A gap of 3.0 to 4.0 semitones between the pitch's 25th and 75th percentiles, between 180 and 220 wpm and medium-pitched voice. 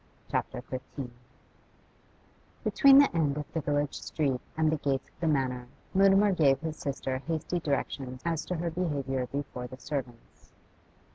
No: average, 3.6 semitones; average, 150 wpm; medium, 145 Hz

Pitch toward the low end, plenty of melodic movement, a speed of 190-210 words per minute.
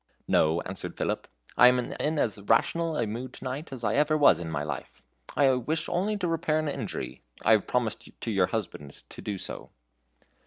Yes: low, 125 Hz; wide, 7.7 semitones; average, 200 wpm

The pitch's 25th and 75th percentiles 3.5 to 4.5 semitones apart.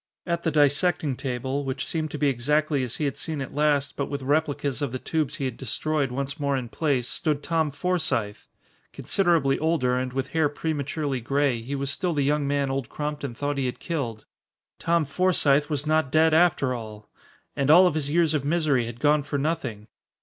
No: average, 2.8 semitones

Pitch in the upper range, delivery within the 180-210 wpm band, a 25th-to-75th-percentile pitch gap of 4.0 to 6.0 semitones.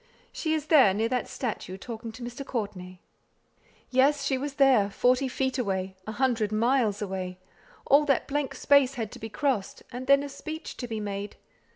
Yes: high, 245 Hz; average, 185 wpm; average, 4.8 semitones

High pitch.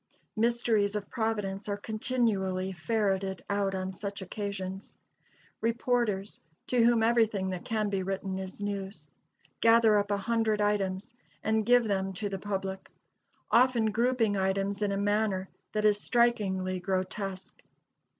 Yes: high, 205 Hz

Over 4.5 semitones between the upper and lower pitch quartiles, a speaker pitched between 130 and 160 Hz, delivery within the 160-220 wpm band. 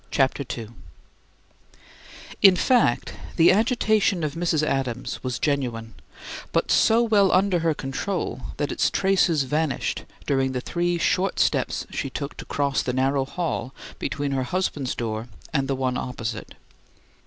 No: wide, 5.5 semitones; medium, 140 Hz; average, 145 wpm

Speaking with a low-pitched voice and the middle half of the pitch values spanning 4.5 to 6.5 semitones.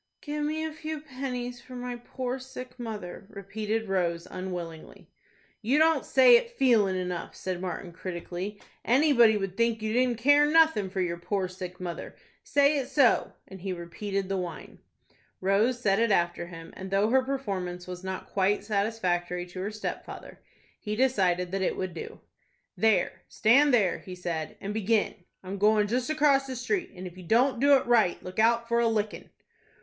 No: high, 210 Hz; wide, 5.5 semitones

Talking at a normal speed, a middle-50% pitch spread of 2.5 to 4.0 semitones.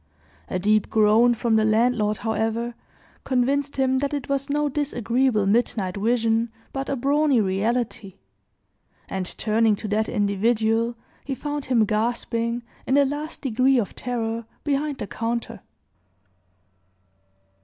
No: slow, 130 wpm; average, 3.5 semitones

